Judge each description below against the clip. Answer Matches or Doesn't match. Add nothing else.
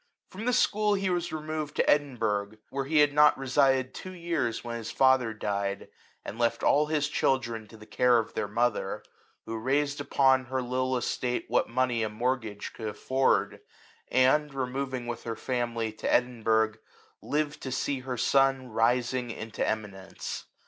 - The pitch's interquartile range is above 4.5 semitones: Doesn't match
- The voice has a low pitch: Matches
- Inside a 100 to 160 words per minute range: Doesn't match